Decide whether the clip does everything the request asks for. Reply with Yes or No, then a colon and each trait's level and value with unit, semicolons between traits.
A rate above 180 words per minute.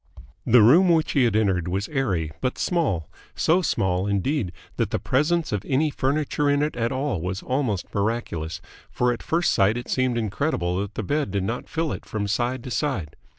Yes: average, 195 wpm